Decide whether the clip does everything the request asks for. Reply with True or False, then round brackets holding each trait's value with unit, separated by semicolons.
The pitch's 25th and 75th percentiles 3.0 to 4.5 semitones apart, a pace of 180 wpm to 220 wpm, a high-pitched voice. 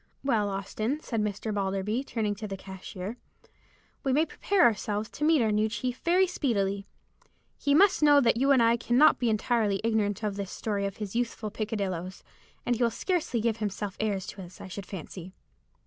True (3.5 semitones; 190 wpm; 215 Hz)